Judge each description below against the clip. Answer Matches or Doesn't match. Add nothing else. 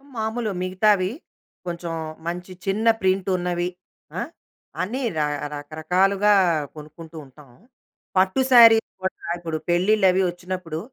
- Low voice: Doesn't match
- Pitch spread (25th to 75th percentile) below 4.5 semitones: Matches